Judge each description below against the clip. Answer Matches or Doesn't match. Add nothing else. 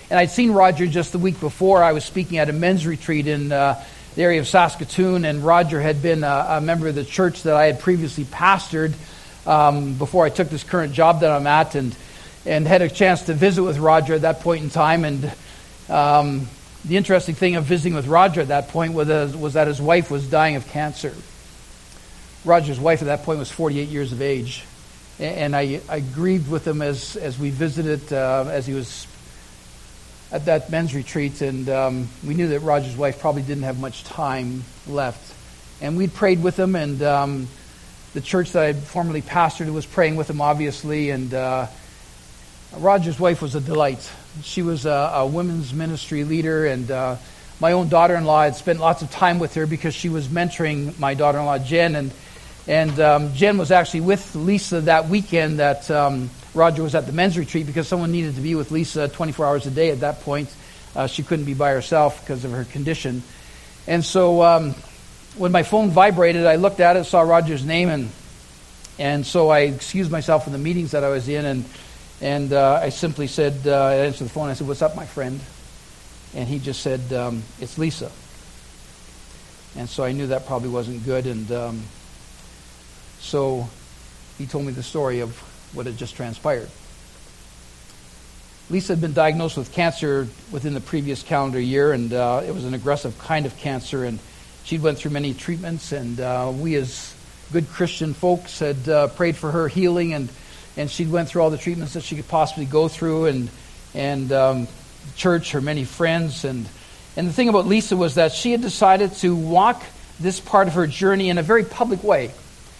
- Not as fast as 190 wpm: Doesn't match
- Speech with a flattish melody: Doesn't match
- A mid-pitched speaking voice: Matches